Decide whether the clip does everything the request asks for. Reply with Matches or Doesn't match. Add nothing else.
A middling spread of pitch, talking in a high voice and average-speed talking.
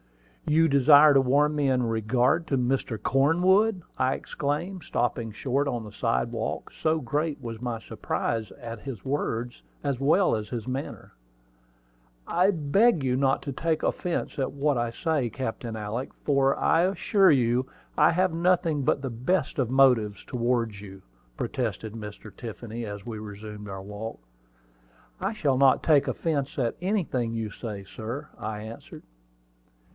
Doesn't match